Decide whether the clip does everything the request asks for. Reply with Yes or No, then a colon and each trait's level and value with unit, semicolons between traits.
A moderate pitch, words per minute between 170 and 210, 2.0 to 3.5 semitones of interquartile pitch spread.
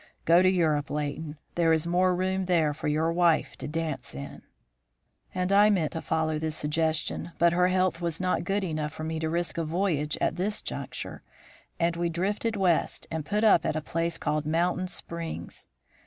Yes: medium, 165 Hz; average, 190 wpm; average, 2.7 semitones